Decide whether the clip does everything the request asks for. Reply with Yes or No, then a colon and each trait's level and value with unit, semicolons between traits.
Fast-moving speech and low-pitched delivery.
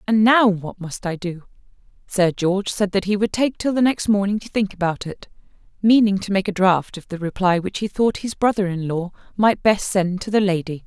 No: fast, 225 wpm; high, 195 Hz